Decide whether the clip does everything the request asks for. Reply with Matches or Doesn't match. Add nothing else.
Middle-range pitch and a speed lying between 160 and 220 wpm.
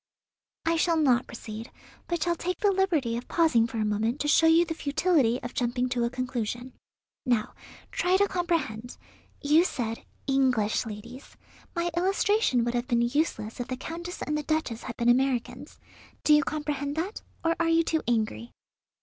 Doesn't match